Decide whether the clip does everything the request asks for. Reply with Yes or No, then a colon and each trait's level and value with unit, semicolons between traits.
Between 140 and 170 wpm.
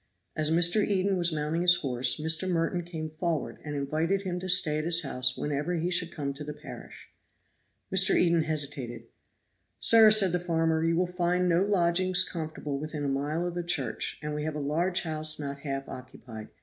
No: average, 195 wpm